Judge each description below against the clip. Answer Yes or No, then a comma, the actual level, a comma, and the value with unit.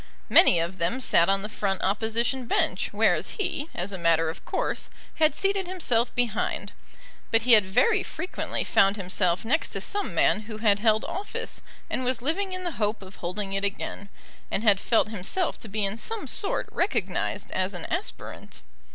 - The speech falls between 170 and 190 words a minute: Yes, average, 185 wpm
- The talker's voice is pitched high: Yes, high, 220 Hz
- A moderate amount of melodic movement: No, wide, 8.0 semitones